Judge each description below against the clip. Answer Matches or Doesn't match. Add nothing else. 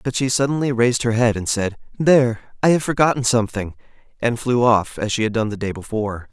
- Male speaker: Matches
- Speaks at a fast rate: Matches